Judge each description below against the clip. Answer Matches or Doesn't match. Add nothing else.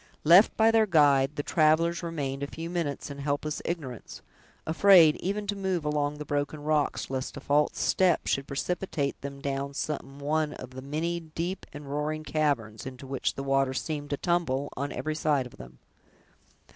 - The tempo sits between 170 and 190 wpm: Matches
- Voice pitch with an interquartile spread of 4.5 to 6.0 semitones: Doesn't match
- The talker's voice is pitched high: Doesn't match